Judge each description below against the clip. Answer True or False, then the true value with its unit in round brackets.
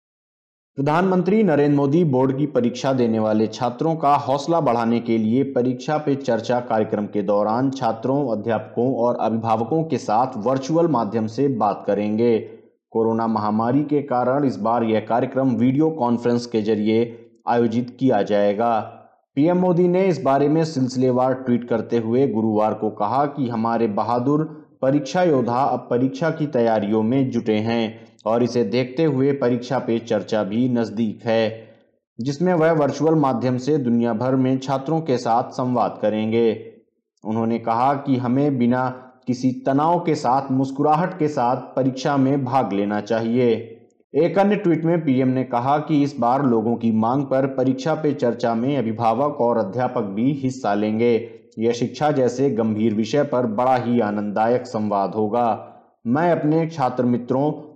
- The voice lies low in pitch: True (125 Hz)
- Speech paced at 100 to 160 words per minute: True (155 wpm)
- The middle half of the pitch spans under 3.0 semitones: False (3.6 semitones)